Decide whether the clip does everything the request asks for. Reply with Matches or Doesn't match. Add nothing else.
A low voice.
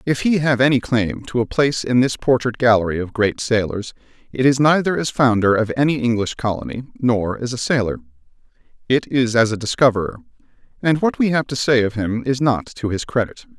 Matches